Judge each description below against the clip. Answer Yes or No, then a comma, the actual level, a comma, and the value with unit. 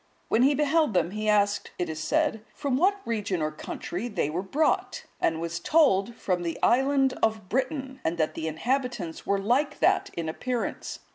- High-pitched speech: Yes, high, 220 Hz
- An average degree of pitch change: No, wide, 7.6 semitones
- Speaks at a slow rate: No, average, 185 wpm